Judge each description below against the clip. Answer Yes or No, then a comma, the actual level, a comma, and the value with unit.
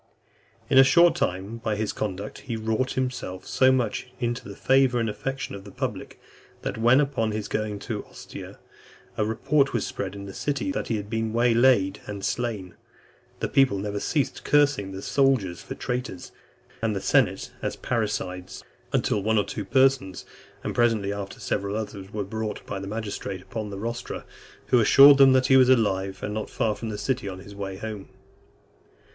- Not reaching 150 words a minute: No, average, 185 wpm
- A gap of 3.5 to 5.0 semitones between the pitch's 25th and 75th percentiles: Yes, average, 4.1 semitones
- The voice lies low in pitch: Yes, low, 110 Hz